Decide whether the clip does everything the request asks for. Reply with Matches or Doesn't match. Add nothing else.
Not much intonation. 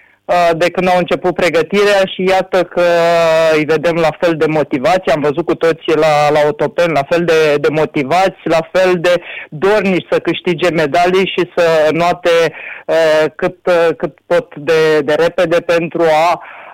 Matches